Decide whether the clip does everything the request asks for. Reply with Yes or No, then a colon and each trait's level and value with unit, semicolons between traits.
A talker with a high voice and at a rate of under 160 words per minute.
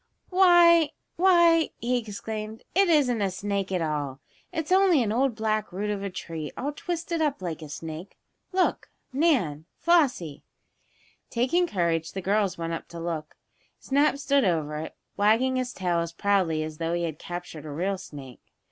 No: high, 205 Hz; average, 170 wpm